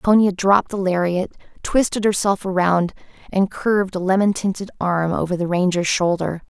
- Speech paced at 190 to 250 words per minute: No, average, 155 wpm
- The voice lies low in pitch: No, high, 190 Hz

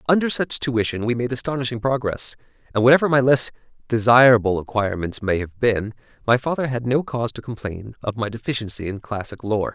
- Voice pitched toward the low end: Yes, low, 120 Hz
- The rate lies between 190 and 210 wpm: No, average, 180 wpm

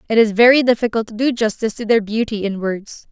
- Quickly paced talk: Yes, fast, 230 wpm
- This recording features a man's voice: No, female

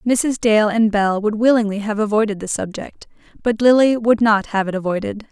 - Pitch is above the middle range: Yes, high, 215 Hz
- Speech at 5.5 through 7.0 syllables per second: No, 5.0 syllables/s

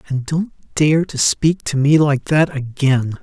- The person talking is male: Yes, male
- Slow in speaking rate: No, average, 185 wpm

